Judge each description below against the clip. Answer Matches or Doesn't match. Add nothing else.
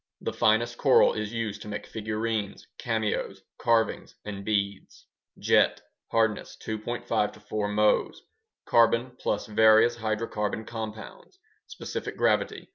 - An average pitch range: Doesn't match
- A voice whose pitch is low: Matches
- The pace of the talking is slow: Matches